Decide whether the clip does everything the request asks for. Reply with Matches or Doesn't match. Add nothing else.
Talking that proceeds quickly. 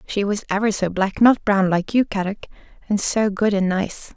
Matches